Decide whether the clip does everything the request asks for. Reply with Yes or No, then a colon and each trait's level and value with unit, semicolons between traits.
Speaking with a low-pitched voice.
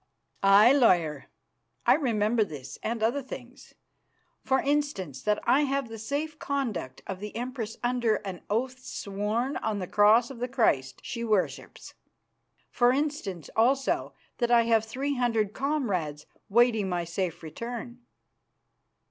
No: high, 230 Hz